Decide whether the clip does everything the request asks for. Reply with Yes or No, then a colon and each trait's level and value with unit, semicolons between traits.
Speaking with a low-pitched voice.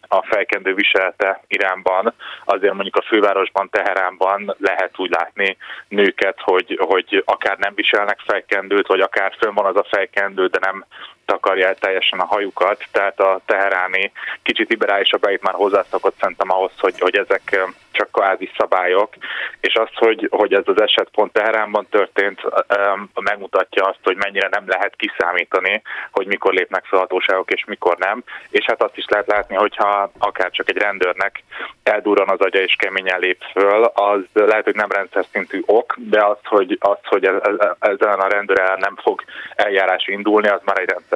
Yes: low, 100 Hz